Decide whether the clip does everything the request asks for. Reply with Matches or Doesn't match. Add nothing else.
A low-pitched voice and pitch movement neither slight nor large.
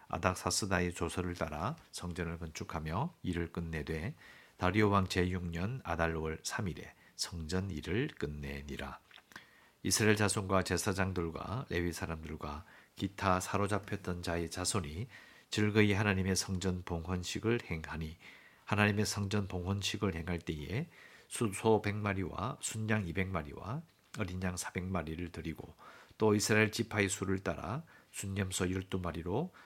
Matches